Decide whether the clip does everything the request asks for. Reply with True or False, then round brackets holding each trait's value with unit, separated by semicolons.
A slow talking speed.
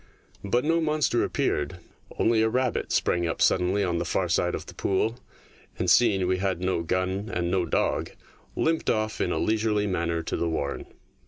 False (185 wpm)